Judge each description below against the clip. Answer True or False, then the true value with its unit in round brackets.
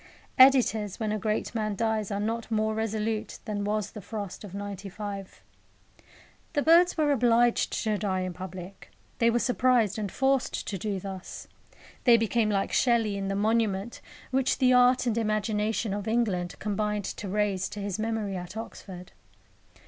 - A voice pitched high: True (215 Hz)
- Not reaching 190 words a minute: True (165 wpm)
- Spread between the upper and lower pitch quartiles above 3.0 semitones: False (2.5 semitones)